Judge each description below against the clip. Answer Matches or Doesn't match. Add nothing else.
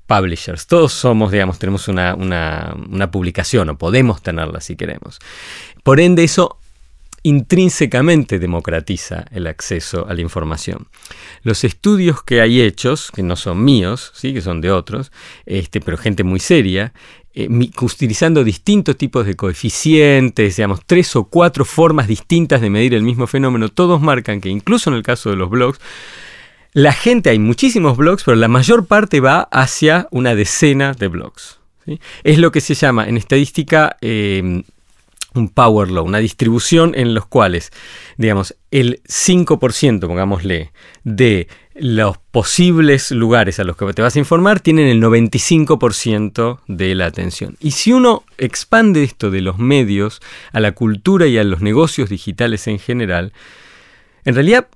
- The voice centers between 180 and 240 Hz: Doesn't match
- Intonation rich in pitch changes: Matches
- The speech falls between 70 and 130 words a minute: Doesn't match